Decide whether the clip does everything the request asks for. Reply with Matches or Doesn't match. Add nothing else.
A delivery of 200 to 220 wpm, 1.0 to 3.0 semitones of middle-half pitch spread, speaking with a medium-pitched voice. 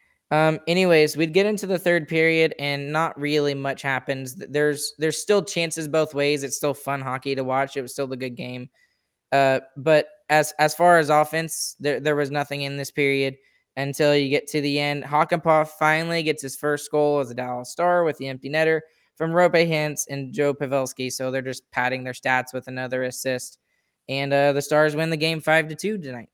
Matches